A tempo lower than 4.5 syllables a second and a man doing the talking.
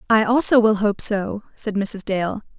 No: 4.3 syllables/s; female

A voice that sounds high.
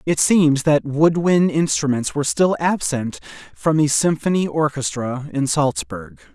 No: medium, 150 Hz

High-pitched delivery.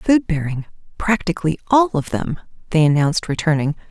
No: medium, 170 Hz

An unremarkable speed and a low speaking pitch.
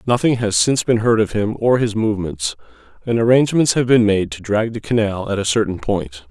No: fast, 220 wpm; low, 110 Hz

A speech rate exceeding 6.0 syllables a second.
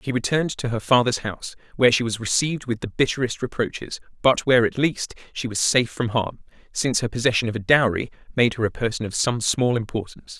Yes: 6.3 syllables/s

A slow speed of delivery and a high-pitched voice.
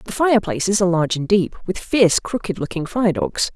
No: fast, 205 wpm; high, 195 Hz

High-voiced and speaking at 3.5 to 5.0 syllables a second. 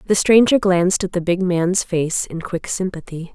No: medium, 180 Hz; 4.7 syllables/s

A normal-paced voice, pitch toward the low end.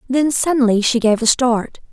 No: average, 190 wpm; high, 245 Hz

